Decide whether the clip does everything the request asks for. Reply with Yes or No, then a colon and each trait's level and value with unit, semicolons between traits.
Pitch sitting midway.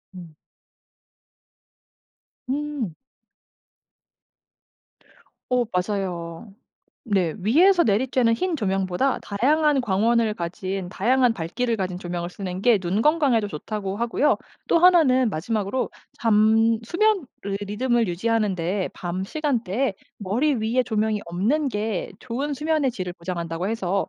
No: high, 220 Hz